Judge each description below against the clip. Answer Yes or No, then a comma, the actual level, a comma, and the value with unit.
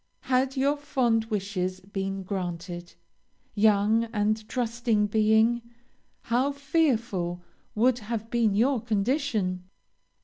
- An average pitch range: Yes, average, 3.7 semitones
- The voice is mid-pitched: No, high, 220 Hz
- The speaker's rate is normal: No, slow, 100 wpm